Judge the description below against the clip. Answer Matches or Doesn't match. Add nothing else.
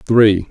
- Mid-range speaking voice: Doesn't match